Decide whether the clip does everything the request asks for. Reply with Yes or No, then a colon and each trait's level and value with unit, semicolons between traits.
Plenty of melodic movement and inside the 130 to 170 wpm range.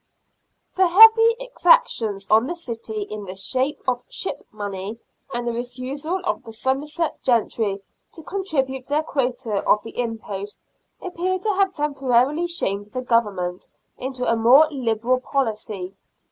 Yes: wide, 6.0 semitones; average, 140 wpm